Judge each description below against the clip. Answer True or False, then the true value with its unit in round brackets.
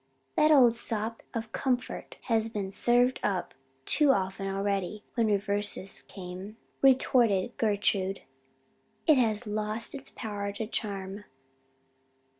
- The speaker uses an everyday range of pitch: True (3.0 semitones)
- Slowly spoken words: True (115 wpm)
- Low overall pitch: False (210 Hz)